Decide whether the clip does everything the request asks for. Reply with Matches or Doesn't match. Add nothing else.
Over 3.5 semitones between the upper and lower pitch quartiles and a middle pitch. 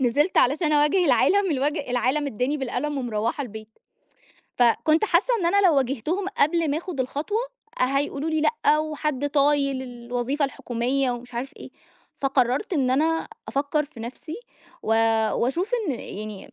Doesn't match